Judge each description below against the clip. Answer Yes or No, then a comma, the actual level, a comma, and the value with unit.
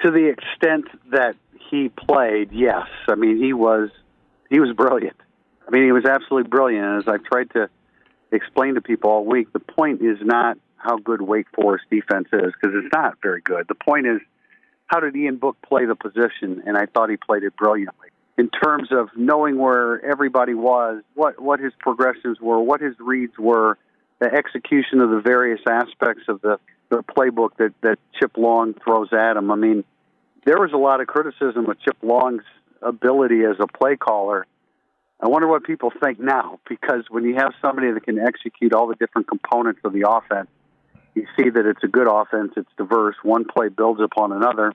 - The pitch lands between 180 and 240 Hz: No, low, 120 Hz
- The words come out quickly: No, average, 195 wpm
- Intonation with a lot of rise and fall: No, average, 3.4 semitones